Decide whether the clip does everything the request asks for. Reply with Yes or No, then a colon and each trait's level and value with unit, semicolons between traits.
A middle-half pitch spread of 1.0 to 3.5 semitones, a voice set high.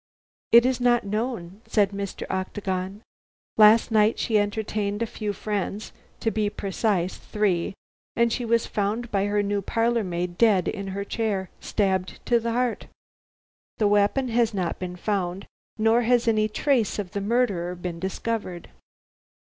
Yes: average, 2.9 semitones; high, 210 Hz